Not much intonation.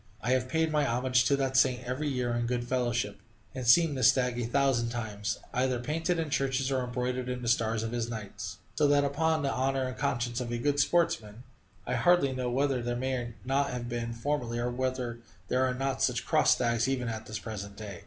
Yes: narrow, 2.3 semitones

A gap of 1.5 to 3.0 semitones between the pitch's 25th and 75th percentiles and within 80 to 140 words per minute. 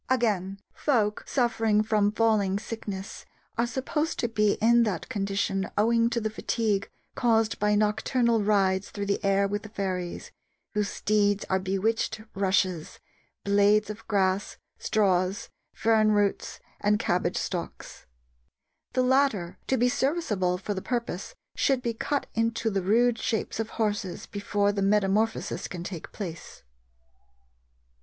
Yes: narrow, 2.5 semitones; slow, 135 wpm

